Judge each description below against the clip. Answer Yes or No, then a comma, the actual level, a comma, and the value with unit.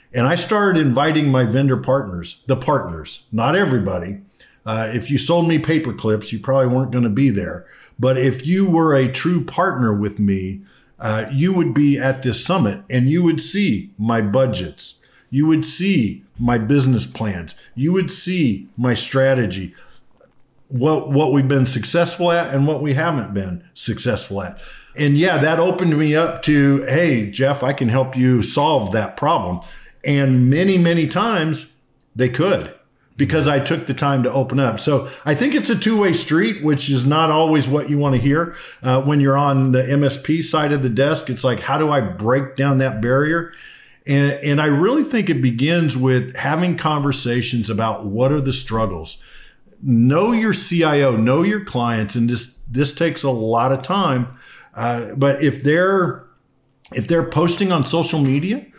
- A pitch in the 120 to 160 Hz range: Yes, medium, 140 Hz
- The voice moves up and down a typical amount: Yes, average, 4.3 semitones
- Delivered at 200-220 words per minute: No, average, 180 wpm